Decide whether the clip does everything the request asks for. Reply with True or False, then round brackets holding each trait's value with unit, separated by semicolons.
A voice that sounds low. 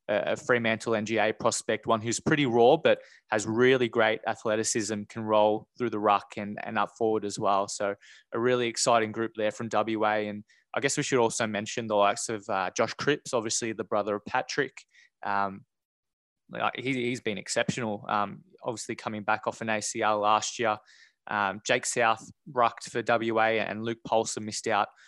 True (110 Hz)